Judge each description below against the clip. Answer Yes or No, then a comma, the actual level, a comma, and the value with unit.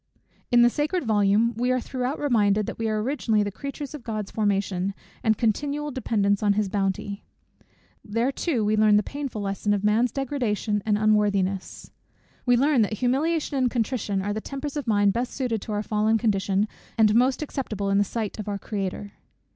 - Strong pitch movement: No, average, 3.7 semitones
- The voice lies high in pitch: Yes, high, 215 Hz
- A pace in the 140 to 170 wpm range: No, average, 185 wpm